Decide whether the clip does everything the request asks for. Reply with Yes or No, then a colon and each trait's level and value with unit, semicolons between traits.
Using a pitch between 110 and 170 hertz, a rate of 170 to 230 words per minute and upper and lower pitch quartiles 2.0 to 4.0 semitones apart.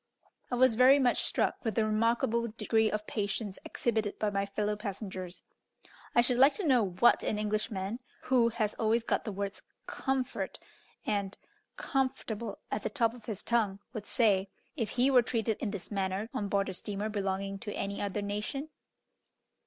No: high, 215 Hz; average, 175 wpm; average, 2.9 semitones